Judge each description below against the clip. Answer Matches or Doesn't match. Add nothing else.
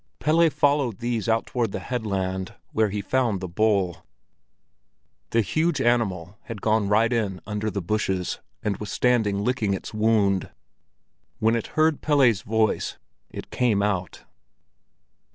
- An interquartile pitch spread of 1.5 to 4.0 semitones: Matches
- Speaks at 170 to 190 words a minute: Doesn't match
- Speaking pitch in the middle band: Doesn't match